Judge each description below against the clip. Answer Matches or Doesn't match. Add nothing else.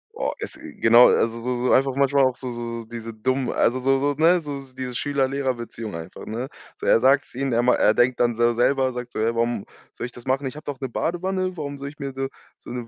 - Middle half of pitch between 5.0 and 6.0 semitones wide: Doesn't match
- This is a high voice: Doesn't match